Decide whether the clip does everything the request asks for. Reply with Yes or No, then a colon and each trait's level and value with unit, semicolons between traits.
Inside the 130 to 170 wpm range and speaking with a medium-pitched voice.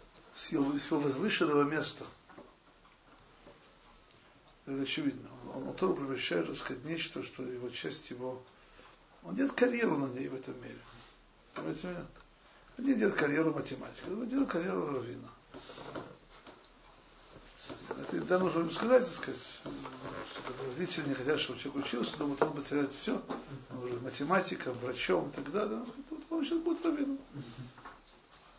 Yes: average, 140 wpm; medium, 155 Hz